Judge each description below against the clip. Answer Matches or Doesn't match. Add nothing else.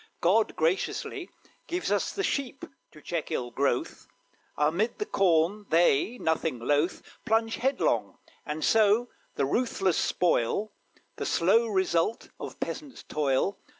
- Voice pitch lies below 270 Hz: Matches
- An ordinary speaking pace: Doesn't match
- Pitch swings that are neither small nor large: Doesn't match